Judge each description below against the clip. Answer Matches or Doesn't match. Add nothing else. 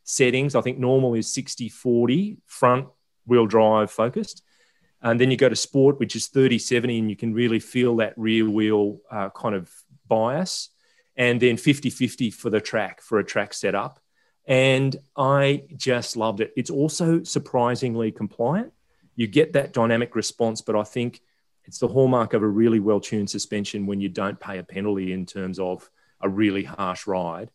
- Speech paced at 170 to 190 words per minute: Matches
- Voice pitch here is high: Doesn't match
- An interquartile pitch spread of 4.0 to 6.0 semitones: Doesn't match